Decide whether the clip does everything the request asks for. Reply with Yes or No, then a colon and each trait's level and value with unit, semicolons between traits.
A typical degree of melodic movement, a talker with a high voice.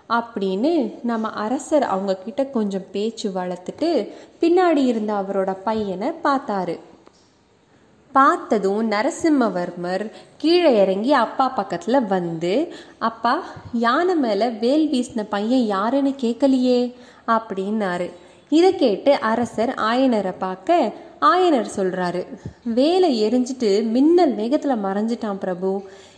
No: wide, 6.0 semitones; high, 230 Hz